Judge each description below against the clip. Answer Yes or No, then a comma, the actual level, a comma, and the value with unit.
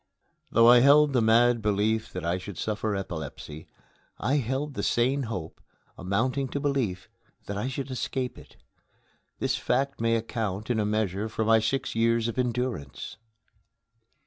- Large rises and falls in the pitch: No, average, 3.8 semitones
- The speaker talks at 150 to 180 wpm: Yes, average, 155 wpm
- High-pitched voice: No, low, 115 Hz